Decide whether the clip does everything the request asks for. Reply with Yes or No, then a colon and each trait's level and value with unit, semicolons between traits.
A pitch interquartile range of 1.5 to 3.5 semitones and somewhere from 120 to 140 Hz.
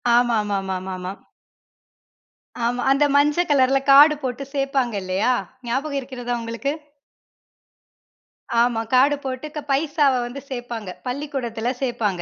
No: average, 3.2 semitones; very high, 250 Hz